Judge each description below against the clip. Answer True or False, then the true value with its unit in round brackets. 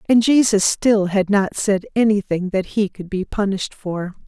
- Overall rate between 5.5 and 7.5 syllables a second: False (4.7 syllables/s)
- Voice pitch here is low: False (200 Hz)